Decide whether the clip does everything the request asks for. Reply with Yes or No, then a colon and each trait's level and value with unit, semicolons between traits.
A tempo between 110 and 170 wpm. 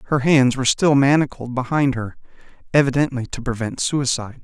Yes: average, 150 wpm